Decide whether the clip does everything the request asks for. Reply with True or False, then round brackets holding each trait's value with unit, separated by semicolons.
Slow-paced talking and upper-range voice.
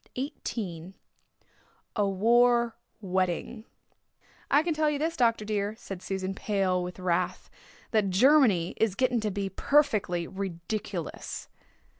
True (125 wpm; 205 Hz)